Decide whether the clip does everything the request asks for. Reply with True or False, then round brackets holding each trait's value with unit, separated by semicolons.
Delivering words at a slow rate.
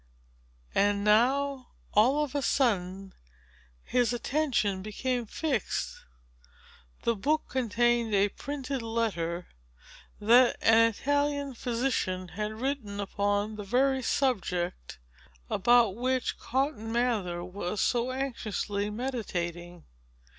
True (100 wpm)